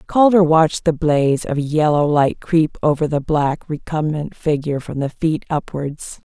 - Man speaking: No, female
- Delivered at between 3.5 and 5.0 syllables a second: Yes, 4.5 syllables/s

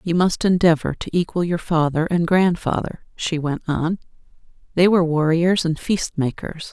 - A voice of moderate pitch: Yes, medium, 170 Hz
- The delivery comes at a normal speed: Yes, average, 160 wpm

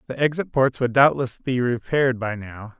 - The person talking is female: No, male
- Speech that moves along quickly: No, average, 195 wpm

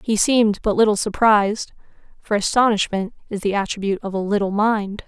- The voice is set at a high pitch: Yes, high, 210 Hz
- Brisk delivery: No, average, 165 wpm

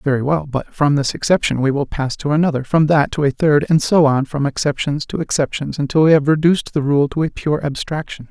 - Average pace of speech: No, fast, 240 wpm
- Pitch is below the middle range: No, medium, 145 Hz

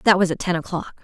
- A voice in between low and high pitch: Yes, medium, 175 Hz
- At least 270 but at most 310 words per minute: Yes, fast, 290 wpm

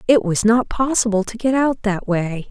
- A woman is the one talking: Yes, female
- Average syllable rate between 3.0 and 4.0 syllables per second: No, 4.7 syllables/s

